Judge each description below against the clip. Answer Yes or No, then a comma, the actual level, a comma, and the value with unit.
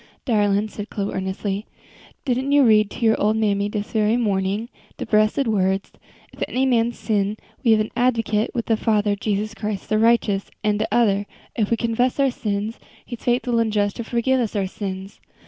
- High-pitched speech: Yes, high, 215 Hz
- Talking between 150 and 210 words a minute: Yes, average, 195 wpm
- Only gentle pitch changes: Yes, narrow, 2.3 semitones